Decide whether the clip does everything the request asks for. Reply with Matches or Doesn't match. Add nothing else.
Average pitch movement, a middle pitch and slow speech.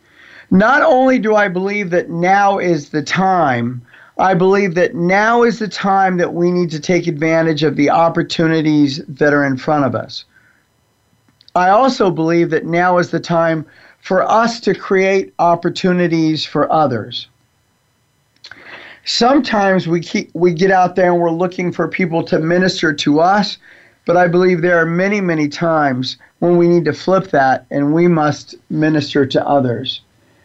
Doesn't match